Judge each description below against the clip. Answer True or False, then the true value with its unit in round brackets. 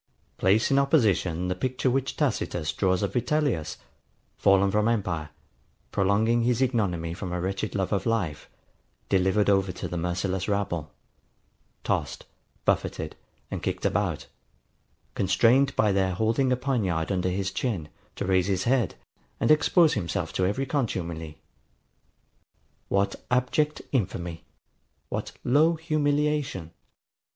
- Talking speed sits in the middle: False (130 wpm)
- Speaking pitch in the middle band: False (100 Hz)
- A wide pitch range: True (5.7 semitones)